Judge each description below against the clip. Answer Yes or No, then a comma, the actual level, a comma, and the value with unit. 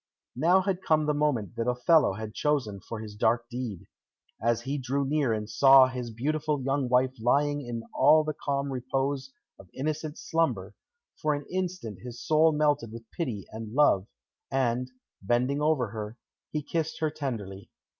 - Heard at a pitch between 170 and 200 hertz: No, low, 135 Hz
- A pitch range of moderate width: Yes, average, 4.4 semitones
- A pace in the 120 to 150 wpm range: No, average, 165 wpm